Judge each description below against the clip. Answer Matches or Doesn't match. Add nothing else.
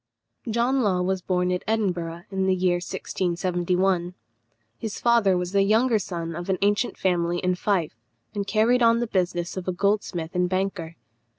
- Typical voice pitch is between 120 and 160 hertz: Doesn't match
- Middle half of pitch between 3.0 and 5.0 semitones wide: Doesn't match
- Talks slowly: Doesn't match